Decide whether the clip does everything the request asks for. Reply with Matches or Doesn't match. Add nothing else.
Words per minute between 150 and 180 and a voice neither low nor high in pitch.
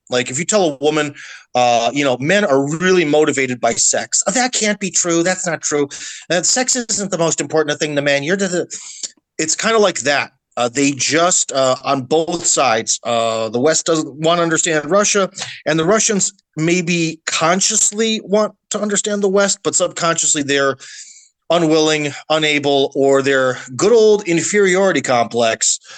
Matches